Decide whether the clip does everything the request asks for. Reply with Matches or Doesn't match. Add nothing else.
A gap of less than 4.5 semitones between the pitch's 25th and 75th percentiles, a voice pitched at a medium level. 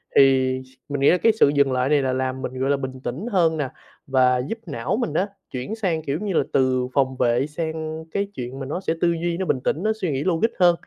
Doesn't match